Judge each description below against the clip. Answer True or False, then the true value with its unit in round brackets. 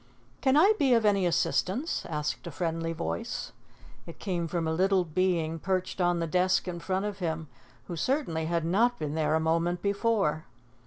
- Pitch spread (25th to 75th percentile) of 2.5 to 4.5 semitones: True (3.2 semitones)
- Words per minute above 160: True (180 wpm)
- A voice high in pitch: False (175 Hz)